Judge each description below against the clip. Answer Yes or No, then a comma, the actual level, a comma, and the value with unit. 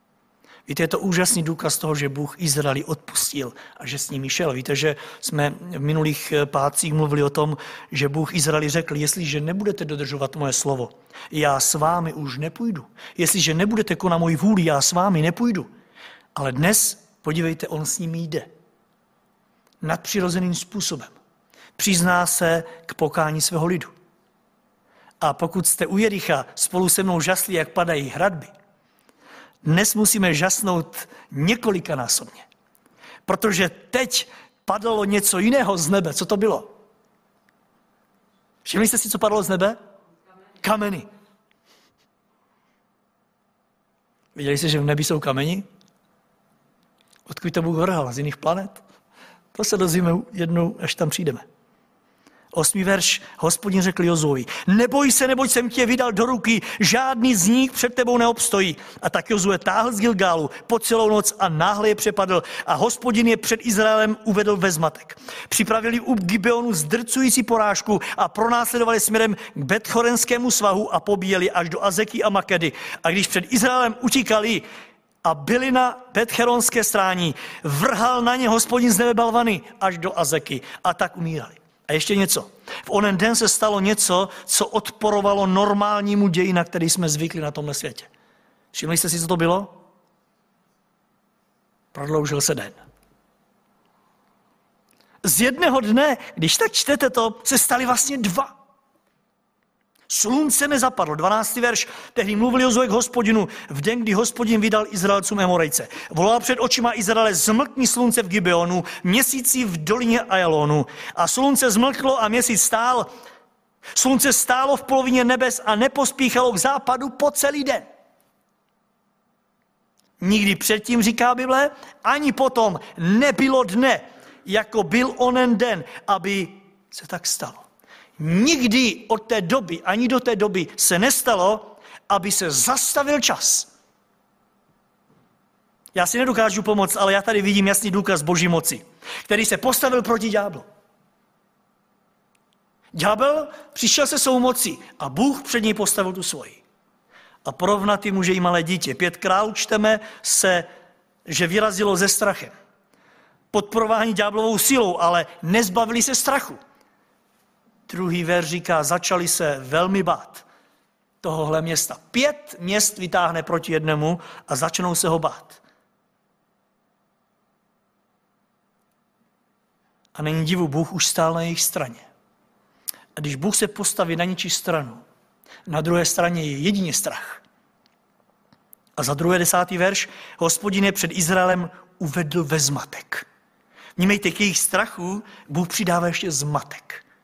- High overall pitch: Yes, high, 205 Hz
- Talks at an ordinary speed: Yes, average, 135 wpm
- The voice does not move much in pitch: No, average, 5.0 semitones